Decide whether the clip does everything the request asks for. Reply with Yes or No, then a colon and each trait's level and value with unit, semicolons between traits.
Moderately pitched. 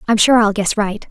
No: high, 210 Hz